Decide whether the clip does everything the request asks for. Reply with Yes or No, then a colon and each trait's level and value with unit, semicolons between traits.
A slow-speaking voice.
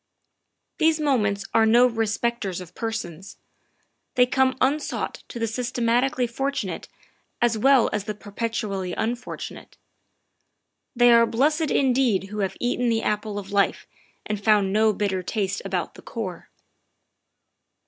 Yes: slow, 130 wpm